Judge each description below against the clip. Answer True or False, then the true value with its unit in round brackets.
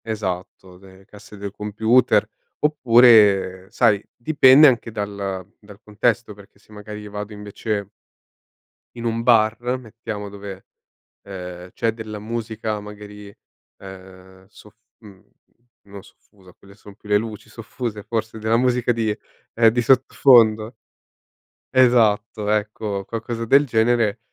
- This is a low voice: True (105 Hz)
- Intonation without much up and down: True (2.3 semitones)